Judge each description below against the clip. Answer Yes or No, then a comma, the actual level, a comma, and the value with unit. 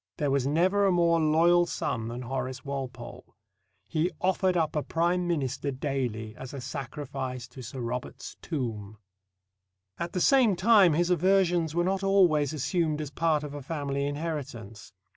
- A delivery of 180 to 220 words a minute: No, average, 160 wpm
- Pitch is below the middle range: No, medium, 150 Hz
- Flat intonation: No, average, 4.9 semitones